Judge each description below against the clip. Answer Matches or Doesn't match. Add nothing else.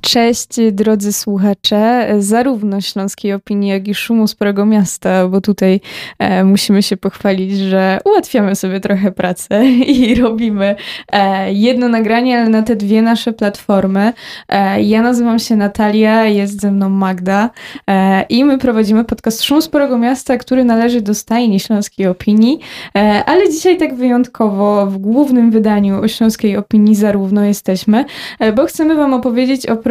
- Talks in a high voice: Matches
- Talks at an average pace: Matches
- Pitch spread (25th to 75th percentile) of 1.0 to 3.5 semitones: Matches